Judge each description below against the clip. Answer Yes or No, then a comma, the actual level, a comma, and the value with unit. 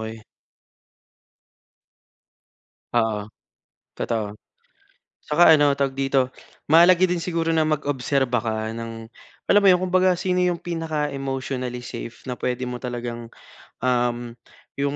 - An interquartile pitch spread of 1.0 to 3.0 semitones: No, wide, 5.4 semitones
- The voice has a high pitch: No, low, 135 Hz